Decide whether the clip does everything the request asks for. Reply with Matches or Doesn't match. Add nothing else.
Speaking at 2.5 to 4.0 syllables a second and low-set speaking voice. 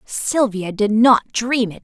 Doesn't match